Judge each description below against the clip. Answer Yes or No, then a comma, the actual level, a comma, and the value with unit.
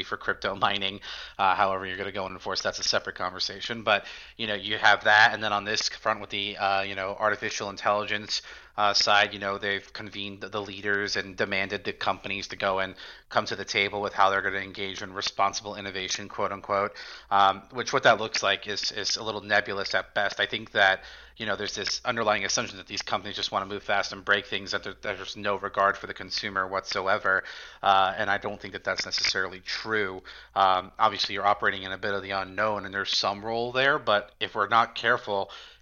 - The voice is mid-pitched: No, low, 100 Hz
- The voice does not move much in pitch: Yes, narrow, 1.1 semitones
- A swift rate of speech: Yes, fast, 225 wpm